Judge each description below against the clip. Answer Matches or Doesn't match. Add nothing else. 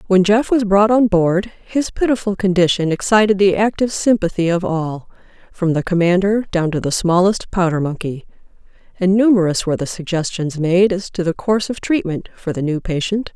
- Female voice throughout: Matches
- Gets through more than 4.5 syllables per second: Matches